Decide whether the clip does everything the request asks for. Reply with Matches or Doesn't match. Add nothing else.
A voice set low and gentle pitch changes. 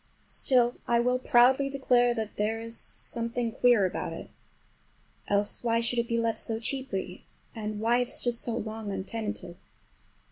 Doesn't match